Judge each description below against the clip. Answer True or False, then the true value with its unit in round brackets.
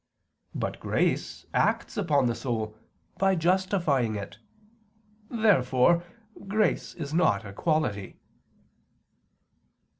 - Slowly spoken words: True (90 wpm)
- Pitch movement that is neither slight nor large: False (8.1 semitones)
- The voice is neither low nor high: True (155 Hz)